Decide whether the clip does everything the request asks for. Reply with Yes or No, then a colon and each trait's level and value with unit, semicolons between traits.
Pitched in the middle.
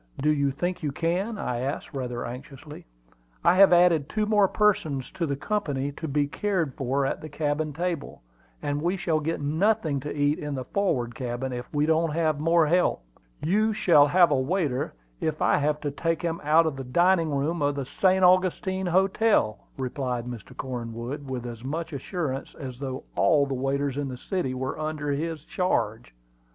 Yes: medium, 150 Hz